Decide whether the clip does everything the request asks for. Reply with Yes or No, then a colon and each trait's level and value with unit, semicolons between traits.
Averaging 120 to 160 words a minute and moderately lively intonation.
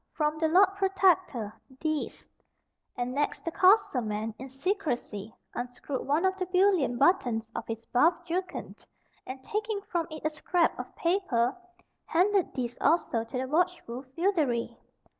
No: average, 145 wpm; wide, 6.8 semitones